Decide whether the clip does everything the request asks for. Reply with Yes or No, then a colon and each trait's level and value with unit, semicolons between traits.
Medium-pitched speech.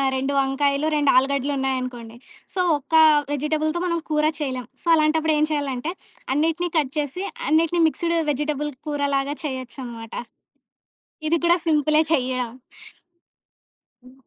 No: very high, 290 Hz